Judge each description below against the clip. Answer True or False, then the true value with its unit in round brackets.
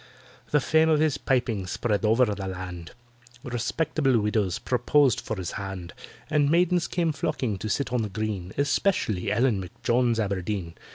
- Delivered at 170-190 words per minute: False (155 wpm)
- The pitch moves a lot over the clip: True (6.3 semitones)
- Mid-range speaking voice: False (115 Hz)